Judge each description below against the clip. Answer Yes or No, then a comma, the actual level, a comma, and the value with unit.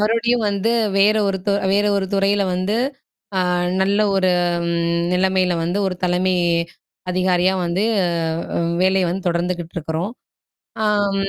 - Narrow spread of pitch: Yes, narrow, 2.0 semitones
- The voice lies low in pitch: No, high, 190 Hz